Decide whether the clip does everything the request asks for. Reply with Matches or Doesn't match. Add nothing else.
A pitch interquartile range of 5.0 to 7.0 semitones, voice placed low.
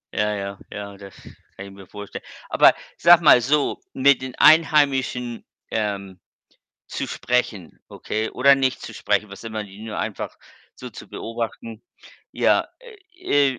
Matches